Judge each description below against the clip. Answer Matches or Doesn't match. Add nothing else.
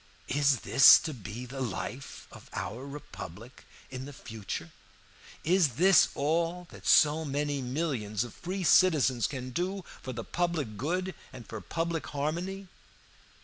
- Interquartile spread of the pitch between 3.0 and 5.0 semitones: Doesn't match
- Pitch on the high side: Doesn't match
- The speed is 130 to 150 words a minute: Matches